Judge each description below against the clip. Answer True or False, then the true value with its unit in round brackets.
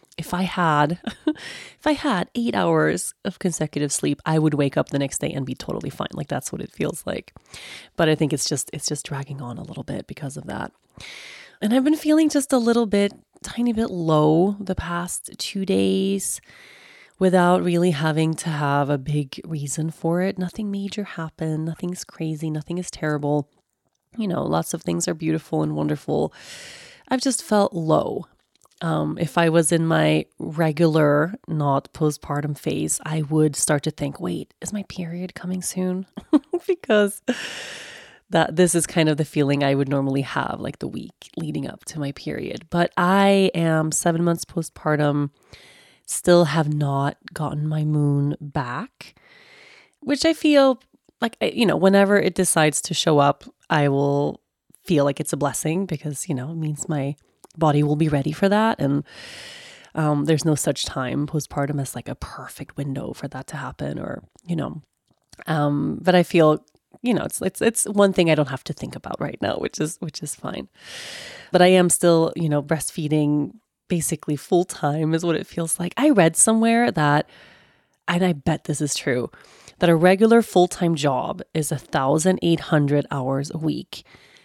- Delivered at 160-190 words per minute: True (180 wpm)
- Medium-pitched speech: True (160 Hz)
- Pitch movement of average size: True (4.0 semitones)